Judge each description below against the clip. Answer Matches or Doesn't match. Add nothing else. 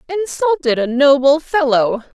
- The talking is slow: Matches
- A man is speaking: Doesn't match